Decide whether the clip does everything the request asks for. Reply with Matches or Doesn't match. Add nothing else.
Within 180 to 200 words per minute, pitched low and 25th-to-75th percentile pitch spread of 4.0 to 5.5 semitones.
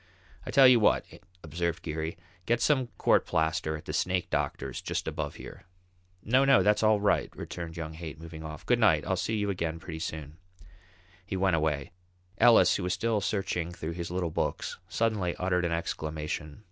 Matches